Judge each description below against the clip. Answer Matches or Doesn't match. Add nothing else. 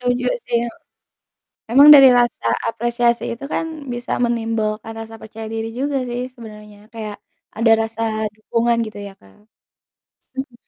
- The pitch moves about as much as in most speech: Doesn't match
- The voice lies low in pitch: Doesn't match